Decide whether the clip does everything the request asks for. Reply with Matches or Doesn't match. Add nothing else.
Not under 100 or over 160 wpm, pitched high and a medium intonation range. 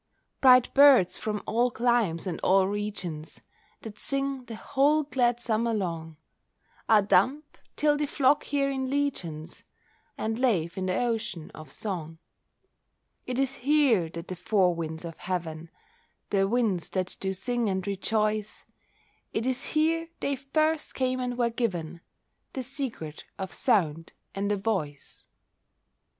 Doesn't match